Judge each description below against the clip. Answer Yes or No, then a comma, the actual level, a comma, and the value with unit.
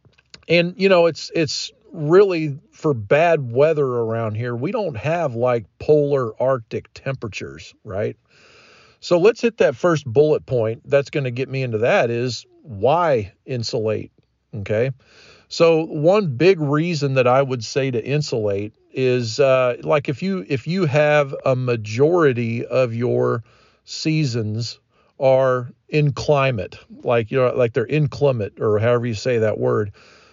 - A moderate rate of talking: Yes, average, 145 wpm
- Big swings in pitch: No, average, 4.3 semitones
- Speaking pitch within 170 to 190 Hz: No, low, 135 Hz